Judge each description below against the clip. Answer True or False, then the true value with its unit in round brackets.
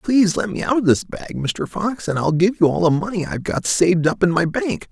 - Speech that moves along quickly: True (280 wpm)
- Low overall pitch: False (180 Hz)